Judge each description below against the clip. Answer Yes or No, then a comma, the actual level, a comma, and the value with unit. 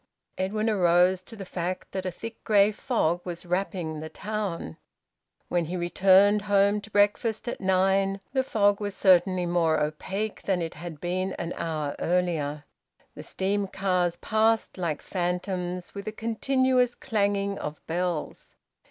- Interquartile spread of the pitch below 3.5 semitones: Yes, average, 2.8 semitones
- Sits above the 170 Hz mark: Yes, high, 190 Hz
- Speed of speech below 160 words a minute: Yes, average, 150 wpm